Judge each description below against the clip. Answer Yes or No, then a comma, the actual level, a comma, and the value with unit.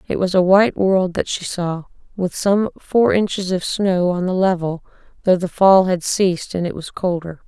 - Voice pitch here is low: No, medium, 185 Hz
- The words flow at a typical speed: No, fast, 210 wpm